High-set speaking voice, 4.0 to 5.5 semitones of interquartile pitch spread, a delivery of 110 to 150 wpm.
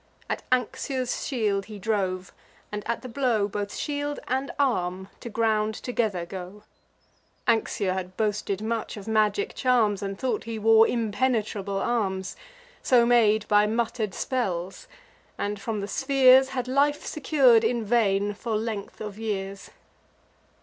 No: high, 220 Hz; average, 3.4 semitones; average, 140 wpm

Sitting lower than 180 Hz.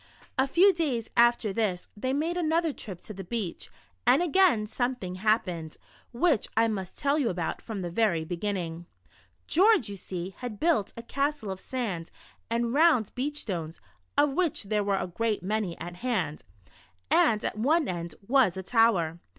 No: high, 220 Hz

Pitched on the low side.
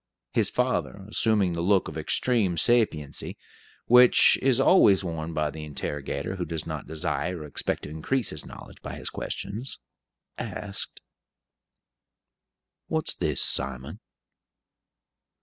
Yes: very low, 85 Hz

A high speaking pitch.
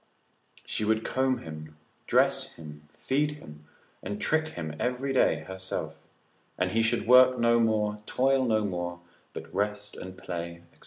No: low, 105 Hz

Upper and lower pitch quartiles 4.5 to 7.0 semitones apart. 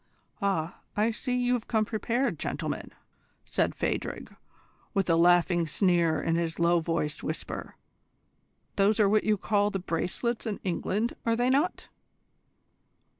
Yes: average, 5.1 semitones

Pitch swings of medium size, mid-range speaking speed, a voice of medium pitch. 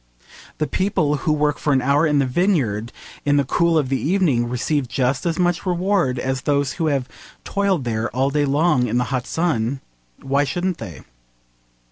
Yes: average, 4.6 semitones; average, 185 wpm; medium, 145 Hz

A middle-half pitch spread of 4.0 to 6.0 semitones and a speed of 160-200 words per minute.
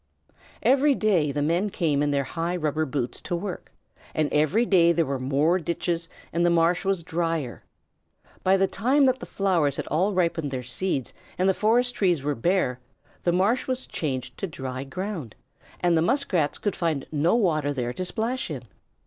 Yes: average, 4.9 semitones; average, 185 wpm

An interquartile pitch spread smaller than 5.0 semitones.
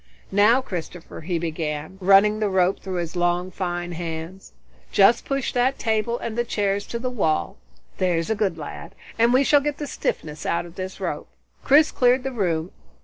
No: average, 5.3 semitones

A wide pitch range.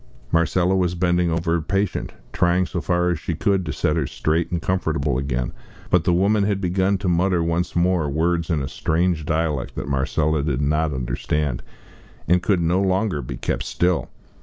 No: average, 2.9 semitones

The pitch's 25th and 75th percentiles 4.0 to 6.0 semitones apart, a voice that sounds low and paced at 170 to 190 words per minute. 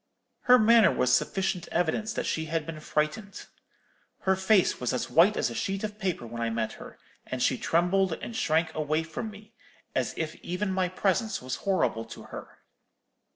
No: average, 4.8 semitones; medium, 180 Hz; average, 185 wpm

